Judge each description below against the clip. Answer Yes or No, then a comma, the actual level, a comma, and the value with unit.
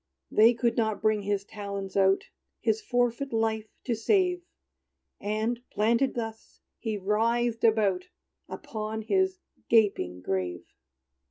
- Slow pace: Yes, slow, 115 wpm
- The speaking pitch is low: No, high, 220 Hz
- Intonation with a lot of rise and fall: No, narrow, 2.4 semitones